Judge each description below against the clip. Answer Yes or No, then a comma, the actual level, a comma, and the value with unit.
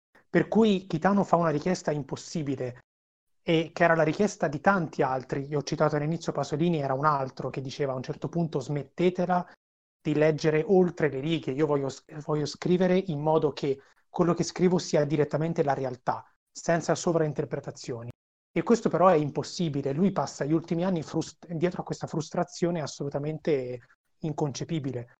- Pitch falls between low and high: Yes, medium, 155 Hz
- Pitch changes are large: No, average, 3.0 semitones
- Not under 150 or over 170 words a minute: Yes, average, 160 wpm